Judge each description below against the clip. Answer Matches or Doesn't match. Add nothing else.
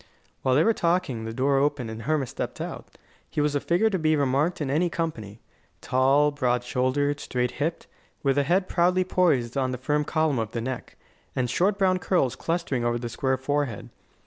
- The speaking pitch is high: Doesn't match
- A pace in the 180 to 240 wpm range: Matches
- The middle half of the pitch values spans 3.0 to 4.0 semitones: Doesn't match